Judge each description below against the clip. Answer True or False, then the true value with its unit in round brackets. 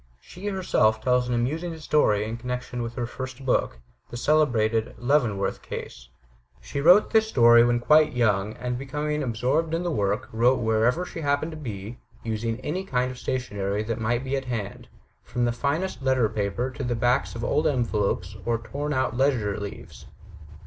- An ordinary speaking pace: True (170 wpm)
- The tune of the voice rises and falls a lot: False (4.3 semitones)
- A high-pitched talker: False (125 Hz)